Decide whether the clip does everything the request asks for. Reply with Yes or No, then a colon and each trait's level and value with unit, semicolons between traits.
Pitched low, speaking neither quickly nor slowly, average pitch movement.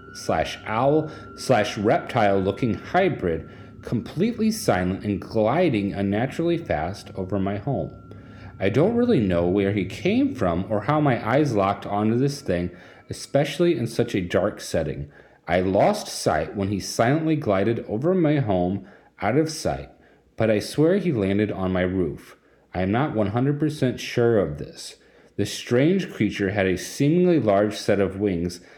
No: low, 105 Hz; average, 155 wpm; wide, 6.9 semitones